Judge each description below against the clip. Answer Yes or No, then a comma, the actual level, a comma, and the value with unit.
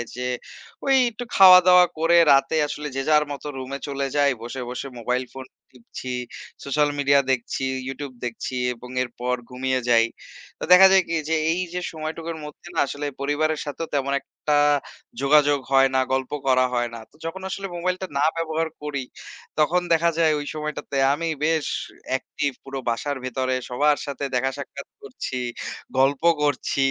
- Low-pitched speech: No, medium, 145 Hz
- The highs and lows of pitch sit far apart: No, average, 3.2 semitones